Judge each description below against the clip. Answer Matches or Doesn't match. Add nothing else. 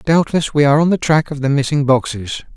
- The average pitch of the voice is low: Doesn't match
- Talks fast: Matches